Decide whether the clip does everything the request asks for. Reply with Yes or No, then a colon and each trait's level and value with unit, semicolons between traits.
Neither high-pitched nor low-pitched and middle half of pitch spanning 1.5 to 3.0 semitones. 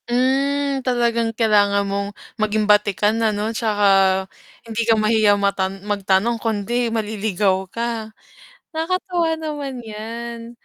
No: high, 220 Hz; narrow, 2.6 semitones